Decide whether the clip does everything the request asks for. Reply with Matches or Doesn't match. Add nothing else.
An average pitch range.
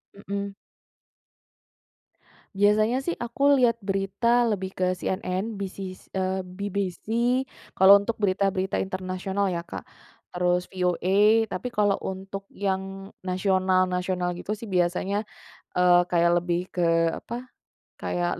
Doesn't match